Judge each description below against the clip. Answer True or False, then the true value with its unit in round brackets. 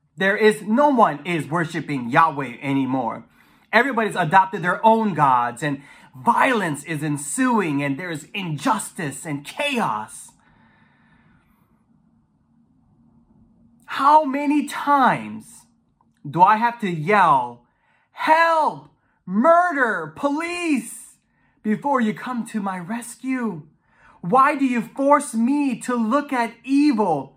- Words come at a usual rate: False (105 wpm)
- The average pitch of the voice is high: True (220 Hz)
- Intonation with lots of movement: True (8.4 semitones)